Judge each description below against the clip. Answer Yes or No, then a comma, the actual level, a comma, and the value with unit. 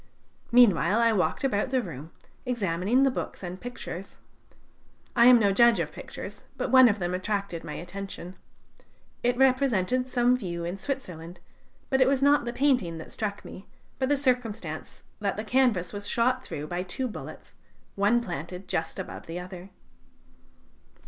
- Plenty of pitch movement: Yes, wide, 5.8 semitones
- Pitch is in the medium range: No, high, 210 Hz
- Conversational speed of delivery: Yes, average, 160 wpm